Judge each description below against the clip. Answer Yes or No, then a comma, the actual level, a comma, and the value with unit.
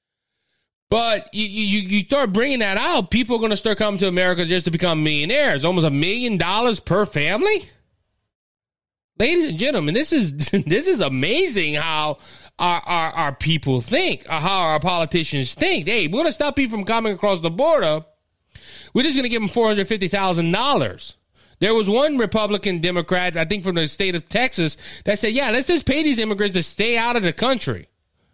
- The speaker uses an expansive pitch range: Yes, wide, 5.8 semitones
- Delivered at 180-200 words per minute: Yes, average, 190 wpm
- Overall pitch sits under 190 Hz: No, high, 200 Hz